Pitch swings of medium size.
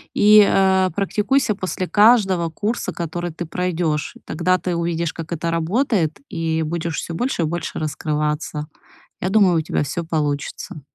Yes: average, 3.0 semitones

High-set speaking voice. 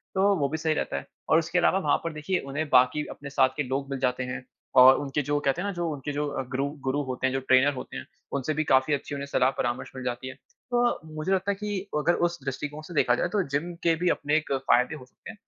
No: medium, 145 Hz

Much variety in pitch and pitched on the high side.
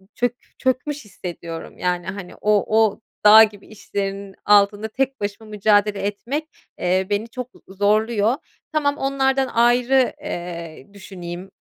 No: average, 4.1 semitones; high, 210 Hz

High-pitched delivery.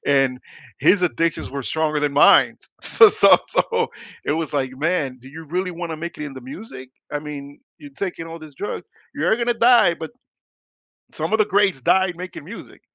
No: medium, 160 Hz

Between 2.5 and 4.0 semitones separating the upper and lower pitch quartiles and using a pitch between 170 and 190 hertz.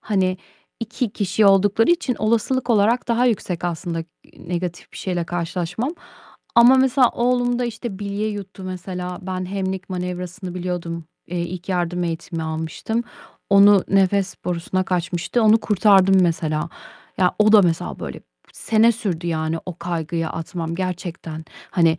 Yes: average, 3.6 semitones; medium, 185 Hz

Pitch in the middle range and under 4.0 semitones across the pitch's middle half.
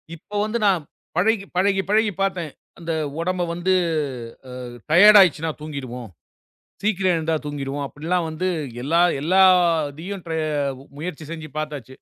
Yes: medium, 170 Hz; average, 3.6 semitones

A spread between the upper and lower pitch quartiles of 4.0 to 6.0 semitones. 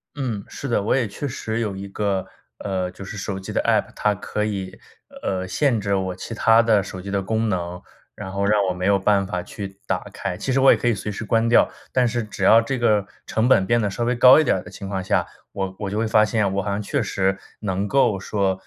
No: average, 2.8 semitones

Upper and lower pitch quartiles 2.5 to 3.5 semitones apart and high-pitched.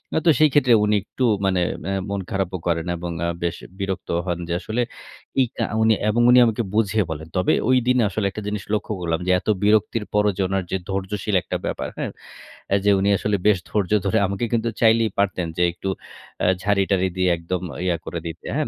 No: average, 3.1 semitones; low, 100 Hz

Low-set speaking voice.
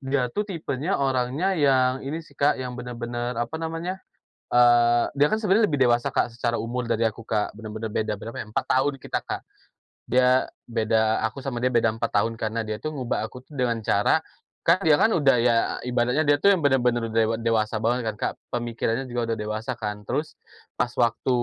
Yes: low, 120 Hz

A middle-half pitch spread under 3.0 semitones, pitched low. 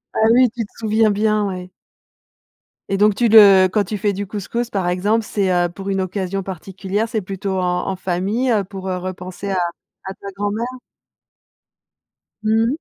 No: narrow, 2.4 semitones; high, 195 Hz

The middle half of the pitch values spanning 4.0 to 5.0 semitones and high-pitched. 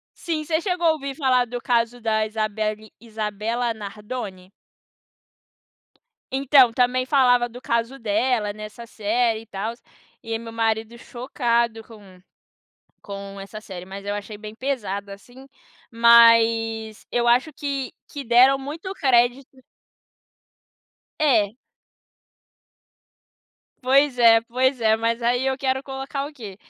No: average, 3.2 semitones; high, 235 Hz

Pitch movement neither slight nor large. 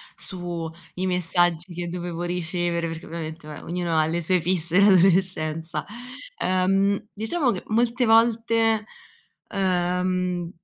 No: narrow, 2.3 semitones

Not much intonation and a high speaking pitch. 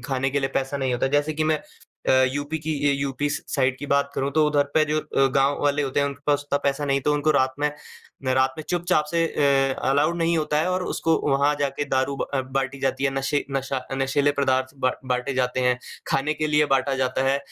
No: narrow, 1.8 semitones; medium, 140 Hz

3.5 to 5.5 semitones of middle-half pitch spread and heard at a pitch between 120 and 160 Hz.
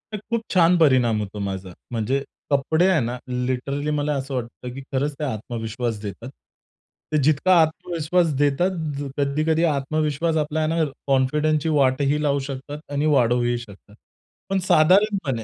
Yes: average, 3.9 semitones; medium, 140 Hz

